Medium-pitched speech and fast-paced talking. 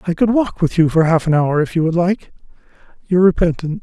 Yes: medium, 170 Hz; fast, 220 wpm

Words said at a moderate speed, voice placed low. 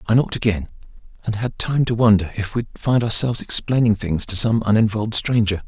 Yes: average, 190 wpm; low, 110 Hz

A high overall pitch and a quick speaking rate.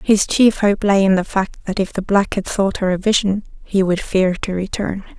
Yes: high, 195 Hz; fast, 245 wpm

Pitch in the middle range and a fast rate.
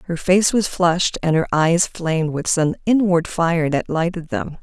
No: medium, 170 Hz; average, 195 wpm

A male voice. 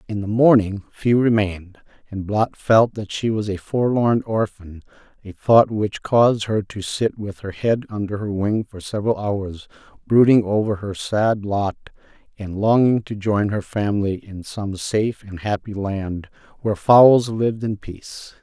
Yes: male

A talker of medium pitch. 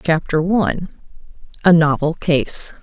Yes: medium, 165 Hz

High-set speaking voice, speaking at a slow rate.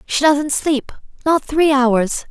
Yes: very high, 280 Hz; slow, 130 wpm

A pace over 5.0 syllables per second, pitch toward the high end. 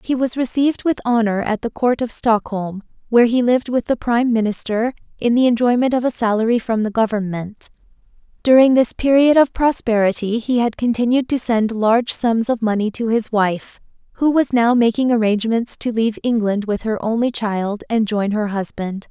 Yes: 5.3 syllables/s; high, 230 Hz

